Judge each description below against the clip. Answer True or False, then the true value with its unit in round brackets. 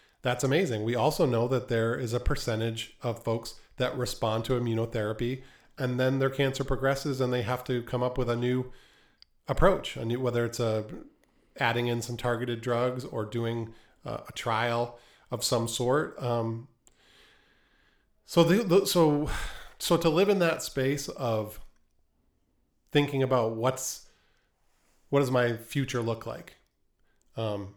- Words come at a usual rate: True (155 wpm)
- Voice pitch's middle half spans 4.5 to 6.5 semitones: False (2.5 semitones)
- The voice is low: True (120 Hz)